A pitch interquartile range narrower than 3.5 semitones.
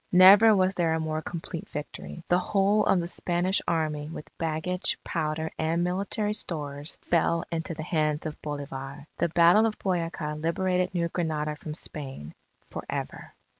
Yes: average, 3.0 semitones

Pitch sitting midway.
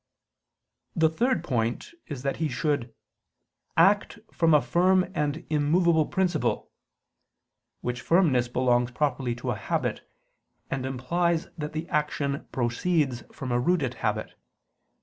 Yes: medium, 150 Hz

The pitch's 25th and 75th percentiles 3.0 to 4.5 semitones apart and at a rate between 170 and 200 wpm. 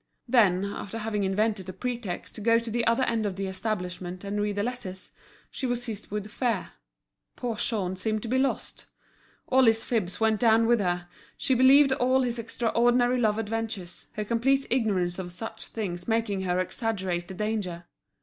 Yes: average, 3.8 semitones; average, 180 wpm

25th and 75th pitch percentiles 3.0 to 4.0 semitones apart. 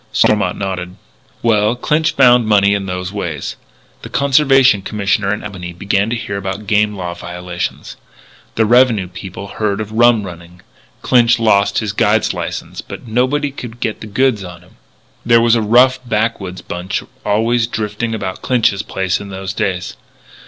Yes: average, 3.6 semitones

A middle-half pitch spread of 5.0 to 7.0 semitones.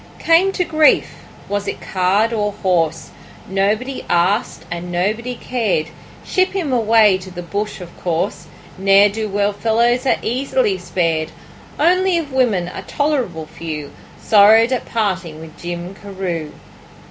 Yes: wide, 5.5 semitones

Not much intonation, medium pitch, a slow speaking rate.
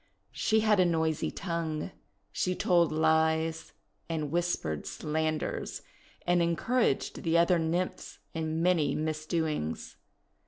Yes: narrow, 1.8 semitones; medium, 160 Hz; slow, 115 wpm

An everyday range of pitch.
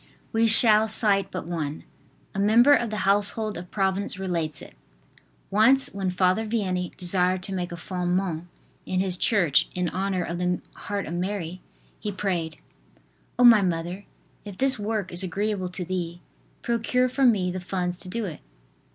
Yes: average, 3.0 semitones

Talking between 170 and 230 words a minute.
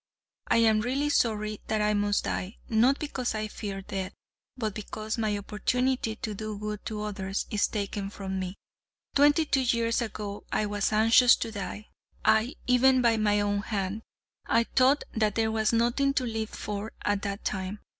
Yes: average, 175 wpm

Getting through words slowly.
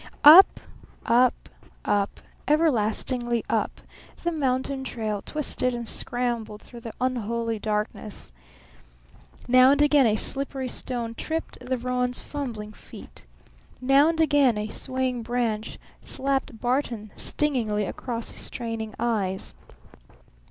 Yes: slow, 115 wpm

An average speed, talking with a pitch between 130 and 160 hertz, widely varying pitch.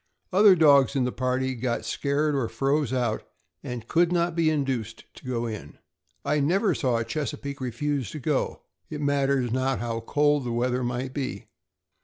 No: average, 175 wpm; low, 135 Hz; average, 3.2 semitones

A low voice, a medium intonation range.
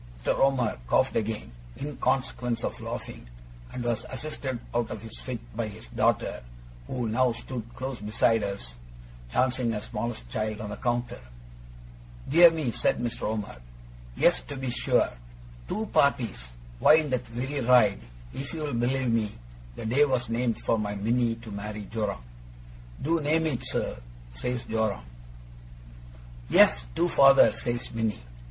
Yes: low, 120 Hz; average, 3.3 semitones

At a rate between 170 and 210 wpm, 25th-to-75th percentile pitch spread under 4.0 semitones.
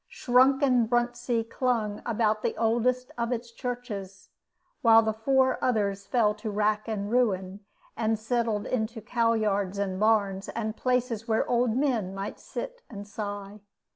No: average, 145 wpm; average, 2.7 semitones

